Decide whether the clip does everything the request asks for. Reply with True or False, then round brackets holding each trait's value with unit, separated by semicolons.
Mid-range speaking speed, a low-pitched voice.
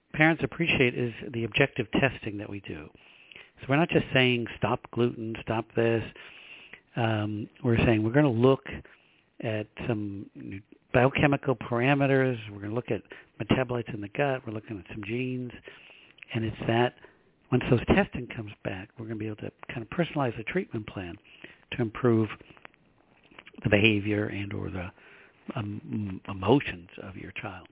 True (160 wpm; 115 Hz)